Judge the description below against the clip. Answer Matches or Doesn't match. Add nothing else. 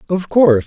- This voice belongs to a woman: Doesn't match